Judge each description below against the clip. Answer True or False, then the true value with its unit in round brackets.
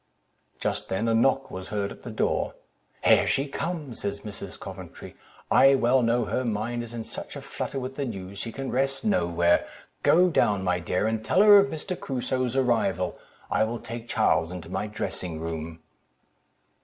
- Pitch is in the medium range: False (115 Hz)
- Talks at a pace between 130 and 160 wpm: False (180 wpm)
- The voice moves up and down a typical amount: False (5.9 semitones)